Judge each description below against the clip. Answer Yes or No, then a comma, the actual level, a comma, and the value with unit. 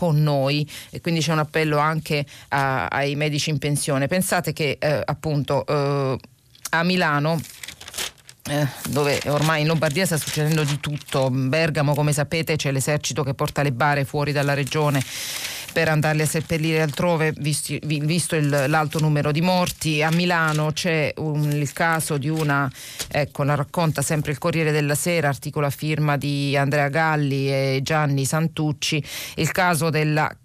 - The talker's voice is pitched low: No, medium, 150 Hz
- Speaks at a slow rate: No, average, 160 wpm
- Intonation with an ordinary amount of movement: No, narrow, 1.9 semitones